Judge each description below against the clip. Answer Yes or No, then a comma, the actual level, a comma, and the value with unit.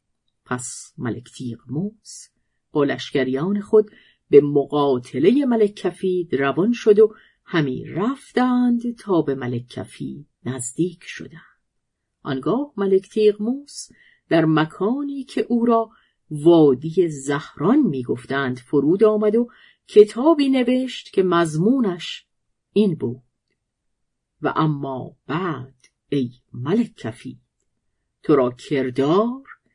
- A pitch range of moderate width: No, wide, 8.3 semitones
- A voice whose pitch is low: No, medium, 170 Hz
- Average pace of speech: No, slow, 100 wpm